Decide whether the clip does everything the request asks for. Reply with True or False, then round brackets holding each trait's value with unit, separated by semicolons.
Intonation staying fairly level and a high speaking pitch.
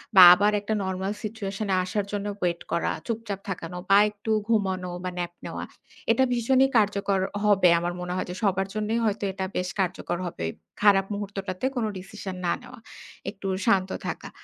True (2.3 semitones; 195 Hz)